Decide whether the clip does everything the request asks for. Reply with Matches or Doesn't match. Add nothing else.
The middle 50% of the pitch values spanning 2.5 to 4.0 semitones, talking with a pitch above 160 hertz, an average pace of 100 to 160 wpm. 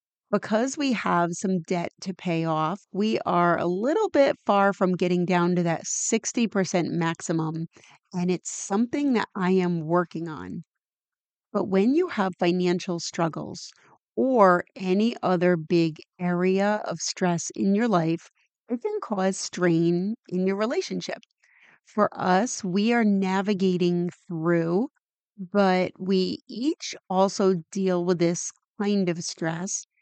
Matches